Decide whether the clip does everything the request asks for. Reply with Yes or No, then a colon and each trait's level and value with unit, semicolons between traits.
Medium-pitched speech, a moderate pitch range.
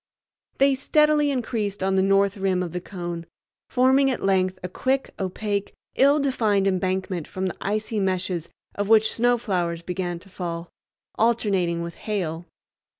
No: high, 195 Hz; average, 3.9 semitones